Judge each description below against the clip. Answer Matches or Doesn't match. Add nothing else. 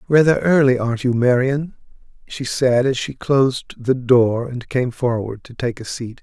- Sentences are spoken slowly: Doesn't match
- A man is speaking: Matches